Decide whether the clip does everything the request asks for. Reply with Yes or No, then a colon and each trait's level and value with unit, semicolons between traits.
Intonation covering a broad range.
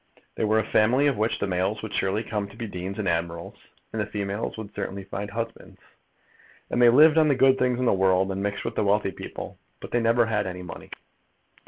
No: average, 3.1 semitones